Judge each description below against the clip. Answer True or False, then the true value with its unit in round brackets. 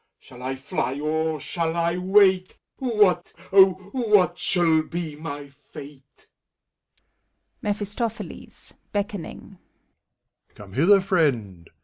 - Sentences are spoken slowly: True (95 wpm)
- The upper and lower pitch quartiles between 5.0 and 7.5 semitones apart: True (5.4 semitones)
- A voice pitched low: False (170 Hz)